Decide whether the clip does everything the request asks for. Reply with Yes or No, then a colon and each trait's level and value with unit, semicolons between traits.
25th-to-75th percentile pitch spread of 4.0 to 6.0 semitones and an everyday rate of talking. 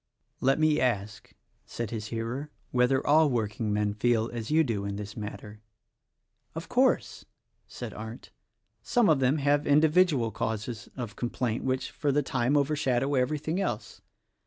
Yes: average, 4.7 semitones; average, 160 wpm